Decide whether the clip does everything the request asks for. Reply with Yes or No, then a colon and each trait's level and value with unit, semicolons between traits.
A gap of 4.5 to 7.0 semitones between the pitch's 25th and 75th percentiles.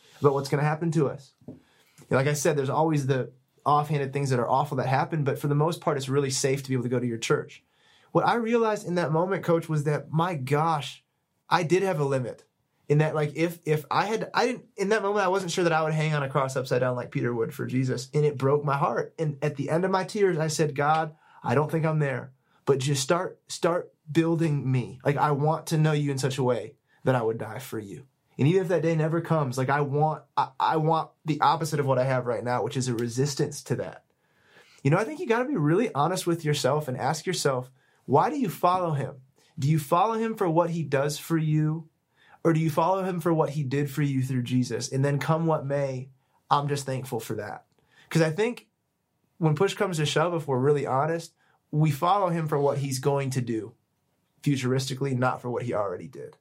No: average, 3.2 semitones